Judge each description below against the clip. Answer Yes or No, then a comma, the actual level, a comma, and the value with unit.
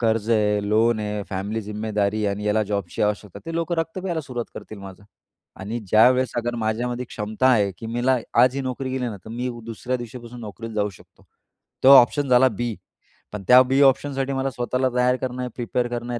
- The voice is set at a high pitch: No, low, 120 Hz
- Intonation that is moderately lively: Yes, average, 3.2 semitones